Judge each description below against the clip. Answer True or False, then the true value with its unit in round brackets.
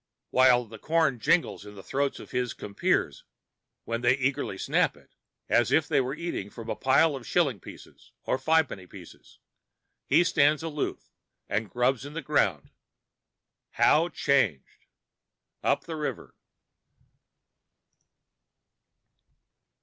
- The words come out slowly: True (125 wpm)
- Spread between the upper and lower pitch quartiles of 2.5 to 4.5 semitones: False (5.2 semitones)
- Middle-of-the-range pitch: False (130 Hz)